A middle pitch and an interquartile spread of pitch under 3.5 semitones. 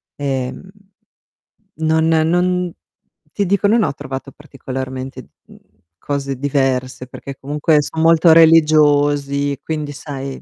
Yes: medium, 145 Hz; average, 2.9 semitones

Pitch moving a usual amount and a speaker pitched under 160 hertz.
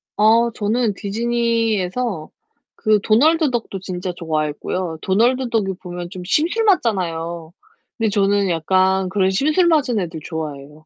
No: average, 4.9 semitones; high, 200 Hz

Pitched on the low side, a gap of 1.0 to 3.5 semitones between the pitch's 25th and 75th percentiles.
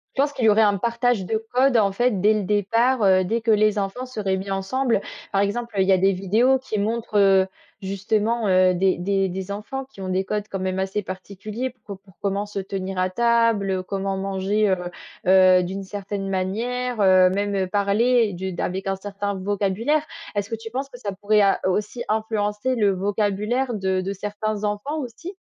No: high, 205 Hz; average, 2.8 semitones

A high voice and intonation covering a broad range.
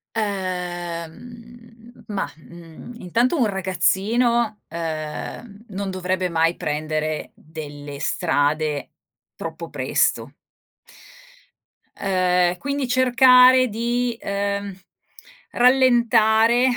Yes: high, 200 Hz; wide, 5.9 semitones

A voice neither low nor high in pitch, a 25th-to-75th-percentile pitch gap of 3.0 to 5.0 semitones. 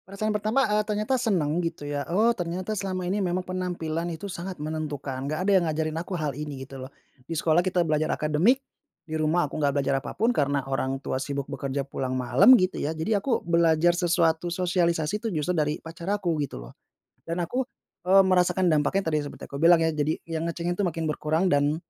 Yes: medium, 165 Hz; average, 3.6 semitones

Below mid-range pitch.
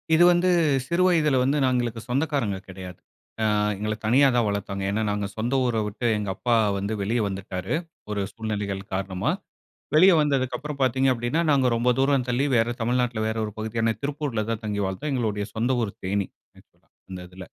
Yes: low, 115 Hz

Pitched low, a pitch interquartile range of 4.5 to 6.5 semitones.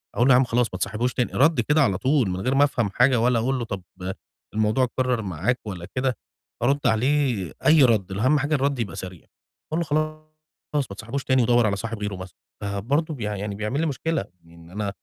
Yes: low, 120 Hz; average, 5.1 semitones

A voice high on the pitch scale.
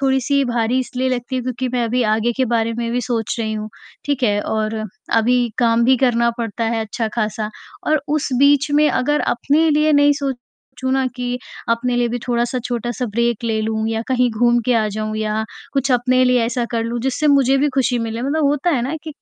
Yes: high, 245 Hz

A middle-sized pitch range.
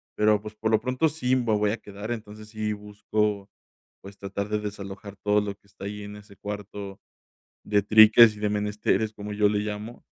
No: narrow, 0.9 semitones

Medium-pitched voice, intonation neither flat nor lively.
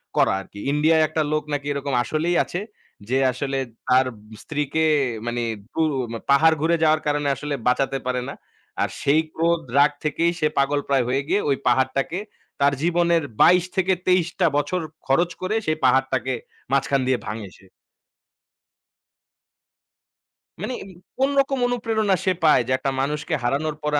Yes: medium, 150 Hz; average, 3.8 semitones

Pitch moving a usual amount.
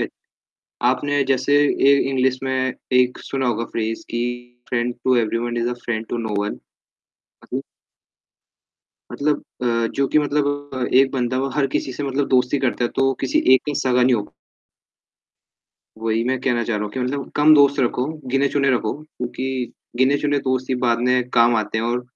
No: narrow, 2.3 semitones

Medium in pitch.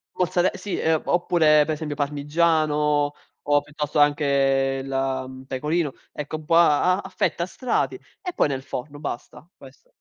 Yes: medium, 150 Hz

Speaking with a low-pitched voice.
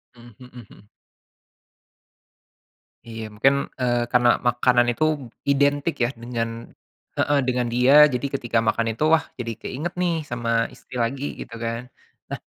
Yes: low, 120 Hz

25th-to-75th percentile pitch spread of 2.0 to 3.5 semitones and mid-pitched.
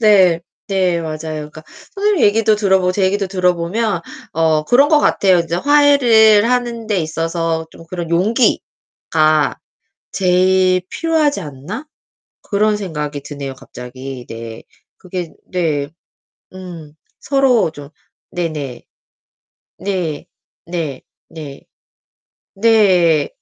No: average, 5.2 semitones; medium, 180 Hz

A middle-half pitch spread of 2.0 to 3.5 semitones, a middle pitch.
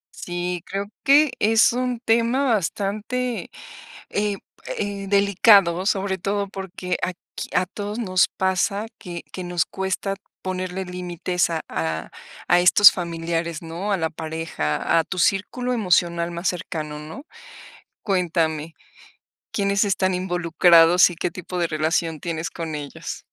Yes: average, 3.0 semitones; medium, 180 Hz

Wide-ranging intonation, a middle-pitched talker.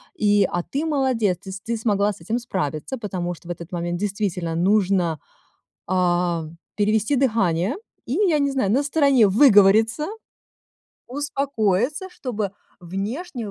No: wide, 6.2 semitones; high, 210 Hz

